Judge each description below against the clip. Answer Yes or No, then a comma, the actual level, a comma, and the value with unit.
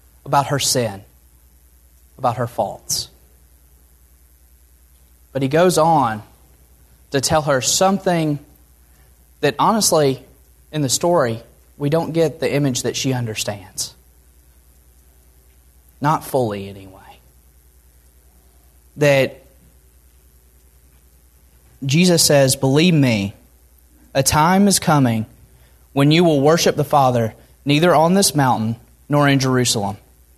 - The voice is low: Yes, very low, 95 Hz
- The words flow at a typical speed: No, slow, 105 wpm